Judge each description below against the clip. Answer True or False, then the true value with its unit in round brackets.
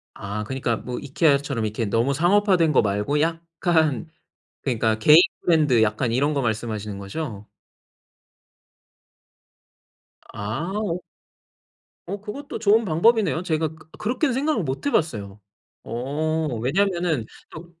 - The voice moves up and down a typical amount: False (7.0 semitones)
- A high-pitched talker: False (150 Hz)